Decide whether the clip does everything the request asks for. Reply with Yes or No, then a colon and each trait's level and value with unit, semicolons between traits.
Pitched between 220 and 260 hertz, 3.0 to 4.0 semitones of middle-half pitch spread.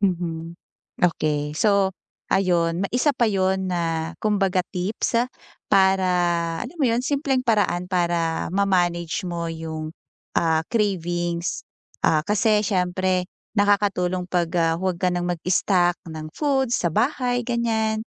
No: medium, 185 Hz; average, 3.7 semitones